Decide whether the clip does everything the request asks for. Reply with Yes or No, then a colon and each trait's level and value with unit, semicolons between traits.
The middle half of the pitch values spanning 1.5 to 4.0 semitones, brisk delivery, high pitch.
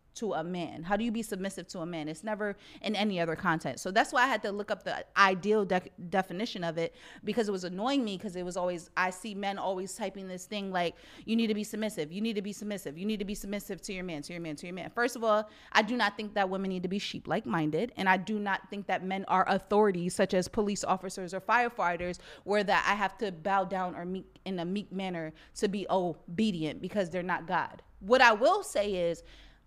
Yes: average, 2.8 semitones; fast, 255 wpm; high, 195 Hz